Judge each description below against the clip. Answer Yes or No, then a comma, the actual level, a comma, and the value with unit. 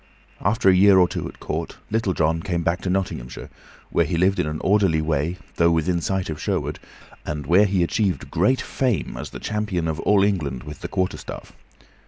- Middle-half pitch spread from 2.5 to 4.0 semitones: Yes, average, 3.4 semitones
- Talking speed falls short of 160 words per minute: No, average, 200 wpm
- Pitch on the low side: Yes, very low, 90 Hz